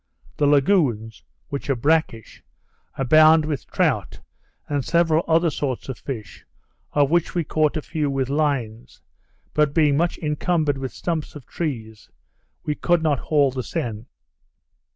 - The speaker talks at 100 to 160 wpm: Yes, average, 145 wpm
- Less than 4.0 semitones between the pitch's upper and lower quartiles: Yes, average, 3.2 semitones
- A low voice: No, medium, 145 Hz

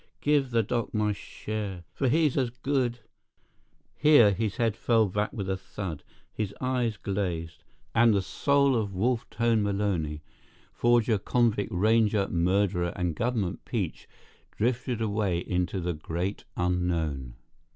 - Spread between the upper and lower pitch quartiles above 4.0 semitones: Yes, average, 4.5 semitones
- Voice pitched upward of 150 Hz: No, low, 105 Hz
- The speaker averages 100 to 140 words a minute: Yes, slow, 135 wpm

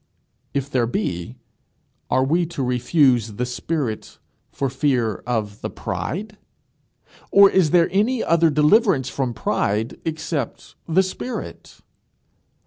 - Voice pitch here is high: No, medium, 140 Hz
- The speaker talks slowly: Yes, slow, 120 wpm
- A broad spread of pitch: Yes, wide, 5.9 semitones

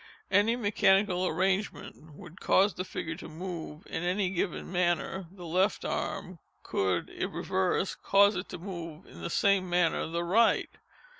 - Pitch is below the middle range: No, medium, 185 Hz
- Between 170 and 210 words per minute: No, average, 155 wpm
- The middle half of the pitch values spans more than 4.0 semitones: No, narrow, 2.4 semitones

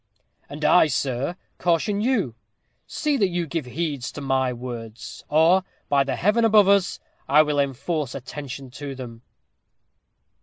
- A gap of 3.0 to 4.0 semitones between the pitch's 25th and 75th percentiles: No, average, 5.2 semitones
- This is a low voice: No, medium, 145 Hz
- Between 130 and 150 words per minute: Yes, average, 145 wpm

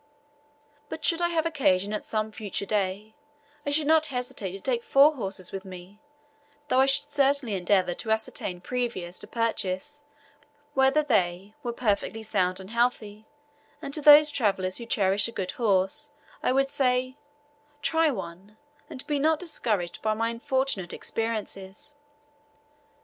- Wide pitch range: Yes, wide, 5.9 semitones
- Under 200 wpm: Yes, average, 150 wpm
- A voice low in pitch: No, high, 225 Hz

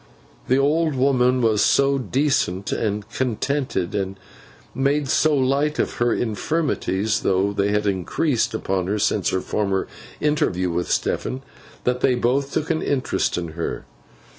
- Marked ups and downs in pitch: Yes, wide, 5.8 semitones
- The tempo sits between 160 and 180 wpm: No, average, 145 wpm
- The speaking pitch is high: No, low, 120 Hz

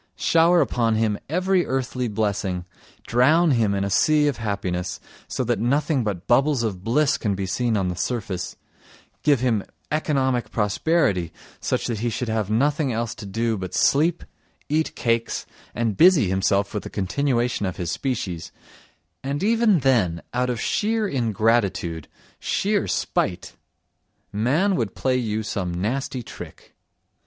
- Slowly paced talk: No, average, 150 wpm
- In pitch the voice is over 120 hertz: No, low, 115 Hz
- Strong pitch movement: Yes, wide, 5.8 semitones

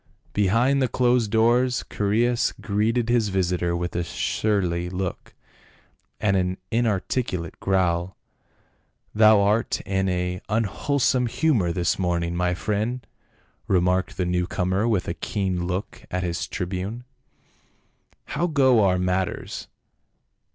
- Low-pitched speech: Yes, very low, 95 Hz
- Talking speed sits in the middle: No, slow, 125 wpm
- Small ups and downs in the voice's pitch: No, average, 4.2 semitones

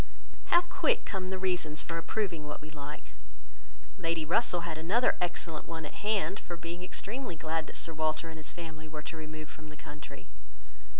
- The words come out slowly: No, average, 185 wpm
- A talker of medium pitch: Yes, medium, 165 Hz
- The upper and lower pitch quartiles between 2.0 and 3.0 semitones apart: Yes, average, 2.7 semitones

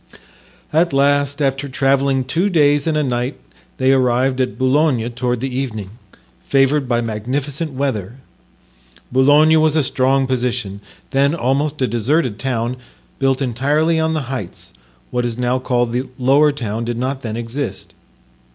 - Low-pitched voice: Yes, low, 130 Hz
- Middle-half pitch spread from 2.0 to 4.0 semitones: Yes, average, 2.7 semitones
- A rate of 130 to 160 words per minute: Yes, average, 150 wpm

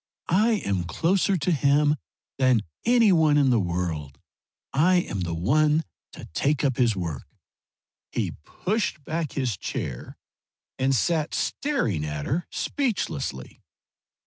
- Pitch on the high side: No, medium, 140 Hz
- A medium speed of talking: No, slow, 130 wpm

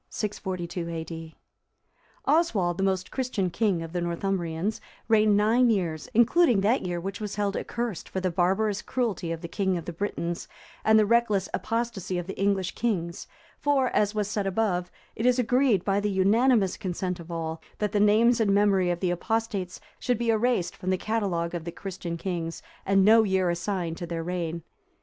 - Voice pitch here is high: Yes, high, 195 Hz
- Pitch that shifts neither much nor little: Yes, average, 3.9 semitones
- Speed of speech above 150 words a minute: Yes, average, 185 wpm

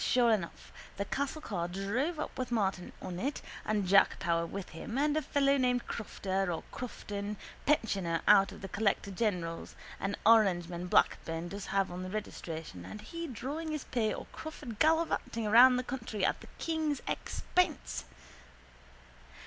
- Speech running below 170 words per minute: Yes, average, 160 wpm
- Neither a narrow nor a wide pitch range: No, wide, 5.8 semitones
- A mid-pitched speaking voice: No, high, 215 Hz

